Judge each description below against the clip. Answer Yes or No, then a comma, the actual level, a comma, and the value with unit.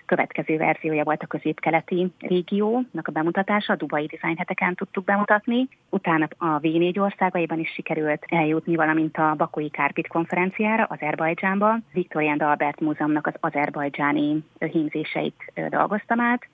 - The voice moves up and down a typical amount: Yes, average, 3.6 semitones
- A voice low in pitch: No, medium, 165 Hz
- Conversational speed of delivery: Yes, average, 125 wpm